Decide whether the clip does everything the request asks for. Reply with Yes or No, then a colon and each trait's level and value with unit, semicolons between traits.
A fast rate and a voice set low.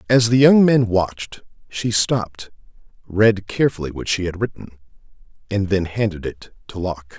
No: average, 160 wpm; low, 100 Hz